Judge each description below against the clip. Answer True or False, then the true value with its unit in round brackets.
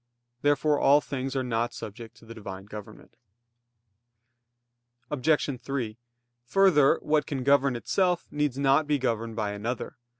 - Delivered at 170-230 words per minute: False (140 wpm)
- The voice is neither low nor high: False (130 Hz)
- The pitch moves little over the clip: False (4.2 semitones)